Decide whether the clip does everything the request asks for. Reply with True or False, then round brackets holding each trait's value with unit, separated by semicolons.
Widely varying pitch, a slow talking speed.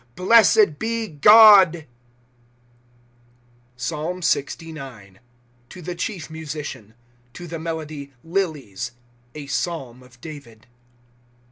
False (4.6 semitones; 95 wpm)